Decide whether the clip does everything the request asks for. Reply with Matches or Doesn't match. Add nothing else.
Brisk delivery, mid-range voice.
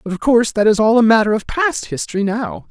Doesn't match